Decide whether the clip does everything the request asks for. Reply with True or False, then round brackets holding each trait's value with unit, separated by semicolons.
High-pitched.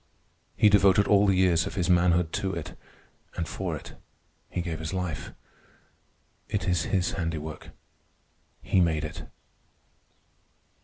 False (90 Hz)